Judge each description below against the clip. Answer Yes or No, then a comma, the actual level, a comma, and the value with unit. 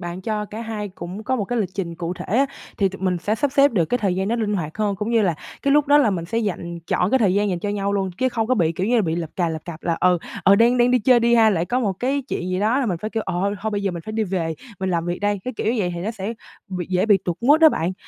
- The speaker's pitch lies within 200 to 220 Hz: Yes, high, 205 Hz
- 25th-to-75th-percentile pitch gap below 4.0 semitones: No, average, 4.4 semitones